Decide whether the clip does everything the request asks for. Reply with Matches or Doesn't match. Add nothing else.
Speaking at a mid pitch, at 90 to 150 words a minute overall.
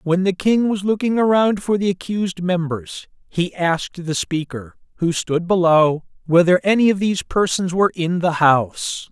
Doesn't match